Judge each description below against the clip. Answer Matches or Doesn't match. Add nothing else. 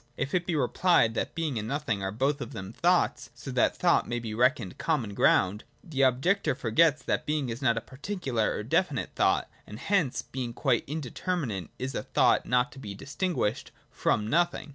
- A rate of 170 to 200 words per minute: Matches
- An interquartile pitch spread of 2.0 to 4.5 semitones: Doesn't match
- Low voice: Matches